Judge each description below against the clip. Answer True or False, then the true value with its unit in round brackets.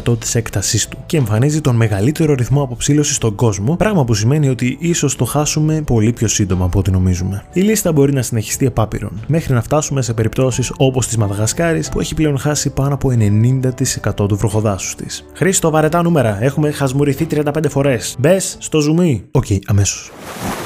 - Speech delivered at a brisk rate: True (175 wpm)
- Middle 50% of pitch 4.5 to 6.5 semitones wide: True (5.2 semitones)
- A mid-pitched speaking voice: False (130 Hz)